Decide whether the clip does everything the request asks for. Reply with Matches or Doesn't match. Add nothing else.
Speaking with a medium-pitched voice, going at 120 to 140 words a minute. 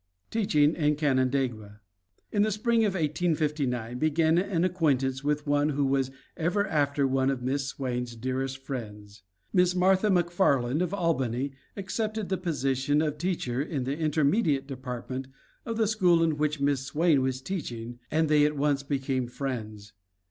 Doesn't match